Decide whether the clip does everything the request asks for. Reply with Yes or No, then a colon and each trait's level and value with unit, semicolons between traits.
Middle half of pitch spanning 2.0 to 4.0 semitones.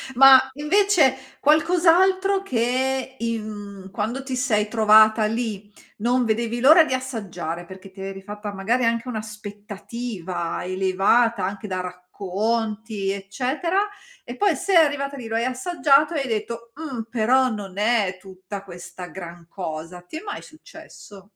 No: average, 5.2 semitones